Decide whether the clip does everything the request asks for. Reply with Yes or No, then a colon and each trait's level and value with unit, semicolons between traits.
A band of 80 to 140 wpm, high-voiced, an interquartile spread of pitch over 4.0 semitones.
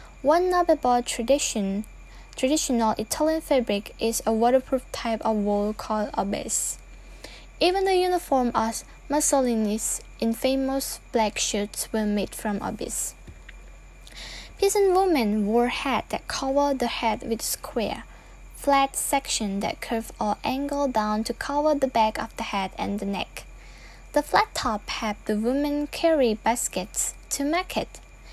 Yes: slow, 135 wpm; high, 245 Hz; average, 4.7 semitones